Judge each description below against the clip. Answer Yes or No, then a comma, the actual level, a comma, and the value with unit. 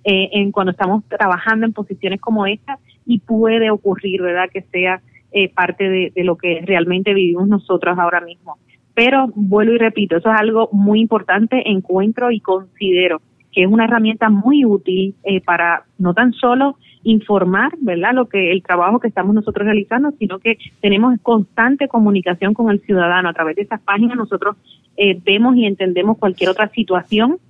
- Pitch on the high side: Yes, high, 200 Hz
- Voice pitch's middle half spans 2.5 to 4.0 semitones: Yes, average, 3.3 semitones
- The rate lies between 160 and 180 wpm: Yes, average, 170 wpm